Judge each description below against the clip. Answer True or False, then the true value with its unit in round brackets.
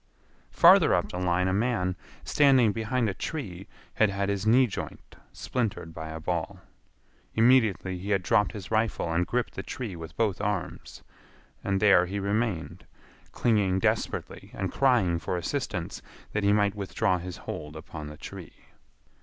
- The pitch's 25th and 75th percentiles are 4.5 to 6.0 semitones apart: False (3.8 semitones)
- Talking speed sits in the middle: True (160 wpm)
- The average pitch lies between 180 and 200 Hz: False (100 Hz)